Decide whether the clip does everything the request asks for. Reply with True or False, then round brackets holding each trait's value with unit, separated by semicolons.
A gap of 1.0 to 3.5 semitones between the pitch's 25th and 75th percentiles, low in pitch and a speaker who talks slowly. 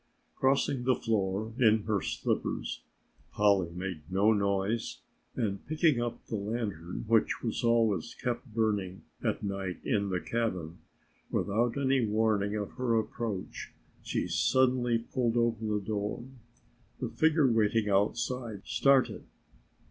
True (3.1 semitones; 110 Hz; 125 wpm)